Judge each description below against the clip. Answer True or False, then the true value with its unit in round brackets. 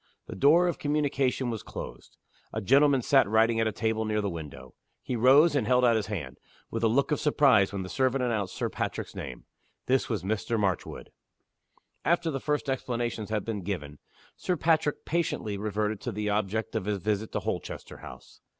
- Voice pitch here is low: True (115 Hz)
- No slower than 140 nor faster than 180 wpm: False (190 wpm)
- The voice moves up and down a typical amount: True (4.7 semitones)